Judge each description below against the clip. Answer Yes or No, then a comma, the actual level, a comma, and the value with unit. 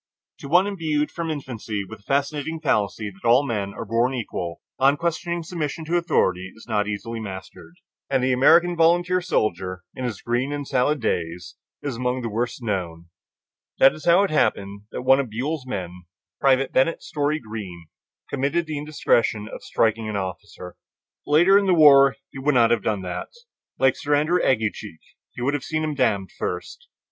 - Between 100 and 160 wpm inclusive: No, average, 180 wpm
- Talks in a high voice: No, low, 130 Hz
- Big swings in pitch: Yes, wide, 6.4 semitones